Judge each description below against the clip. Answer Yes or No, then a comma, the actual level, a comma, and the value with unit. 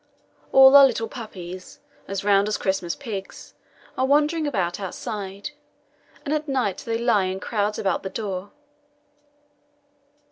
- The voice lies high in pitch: Yes, high, 210 Hz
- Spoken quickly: No, slow, 135 wpm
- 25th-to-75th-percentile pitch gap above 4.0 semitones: Yes, wide, 5.5 semitones